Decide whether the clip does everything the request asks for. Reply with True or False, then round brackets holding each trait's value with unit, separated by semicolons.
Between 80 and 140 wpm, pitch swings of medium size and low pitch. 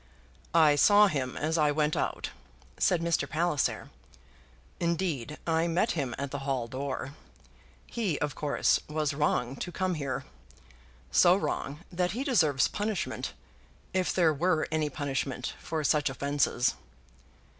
False (135 wpm; 3.8 semitones; 155 Hz)